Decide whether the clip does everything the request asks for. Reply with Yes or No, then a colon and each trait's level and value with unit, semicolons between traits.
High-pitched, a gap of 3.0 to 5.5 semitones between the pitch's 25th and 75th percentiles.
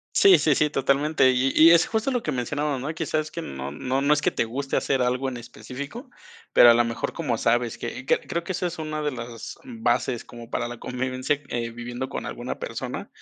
No: low, 135 Hz; average, 4.2 semitones